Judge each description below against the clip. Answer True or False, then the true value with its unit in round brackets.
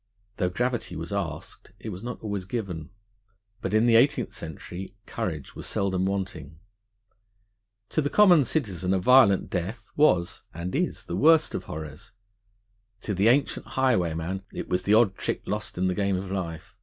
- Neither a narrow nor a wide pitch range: True (4.9 semitones)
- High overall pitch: False (95 Hz)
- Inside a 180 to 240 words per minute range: False (170 wpm)